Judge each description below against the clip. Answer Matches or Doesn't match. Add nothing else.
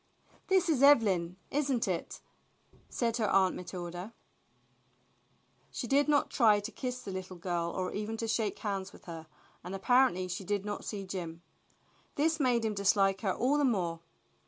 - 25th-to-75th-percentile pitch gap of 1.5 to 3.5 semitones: Doesn't match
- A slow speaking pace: Doesn't match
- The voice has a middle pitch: Doesn't match